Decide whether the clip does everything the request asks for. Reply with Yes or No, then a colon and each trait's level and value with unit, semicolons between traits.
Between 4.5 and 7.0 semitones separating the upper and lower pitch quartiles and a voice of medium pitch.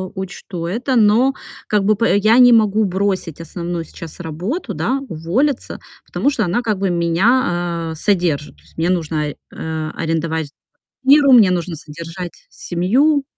Yes: average, 5.3 semitones; medium, 180 Hz